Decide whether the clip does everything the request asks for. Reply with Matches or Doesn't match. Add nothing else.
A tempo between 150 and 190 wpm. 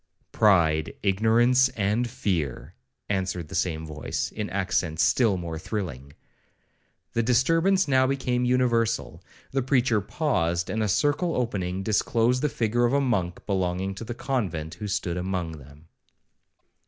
Doesn't match